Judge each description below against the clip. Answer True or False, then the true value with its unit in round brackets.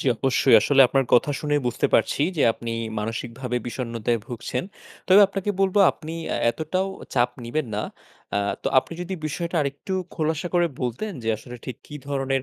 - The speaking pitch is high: False (135 Hz)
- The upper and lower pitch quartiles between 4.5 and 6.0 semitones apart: True (4.9 semitones)